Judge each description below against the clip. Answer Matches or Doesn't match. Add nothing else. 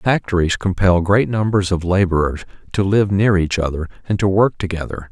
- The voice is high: Doesn't match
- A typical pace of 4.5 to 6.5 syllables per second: Matches